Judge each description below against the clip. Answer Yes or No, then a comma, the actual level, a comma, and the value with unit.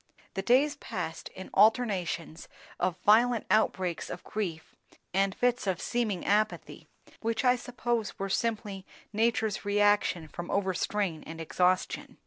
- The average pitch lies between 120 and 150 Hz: No, high, 205 Hz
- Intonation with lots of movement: No, average, 3.8 semitones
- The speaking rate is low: Yes, slow, 125 wpm